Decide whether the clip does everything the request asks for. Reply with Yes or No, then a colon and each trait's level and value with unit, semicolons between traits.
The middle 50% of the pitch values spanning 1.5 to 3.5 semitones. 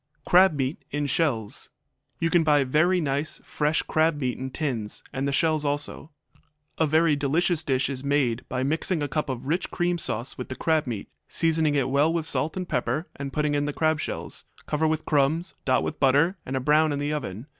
Yes: average, 2.9 semitones